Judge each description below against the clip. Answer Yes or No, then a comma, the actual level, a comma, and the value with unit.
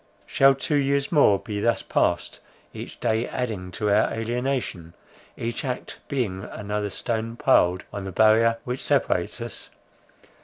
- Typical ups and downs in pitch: Yes, average, 3.7 semitones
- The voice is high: No, low, 115 Hz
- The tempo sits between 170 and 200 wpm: No, average, 145 wpm